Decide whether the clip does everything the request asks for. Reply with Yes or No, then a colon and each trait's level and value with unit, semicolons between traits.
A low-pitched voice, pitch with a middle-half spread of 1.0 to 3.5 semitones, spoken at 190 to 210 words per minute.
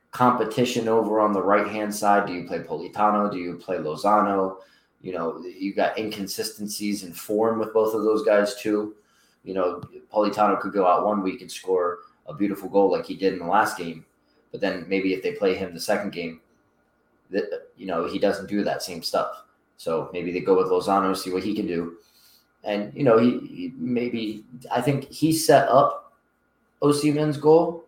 No: low, 105 Hz; average, 4.3 semitones; average, 200 wpm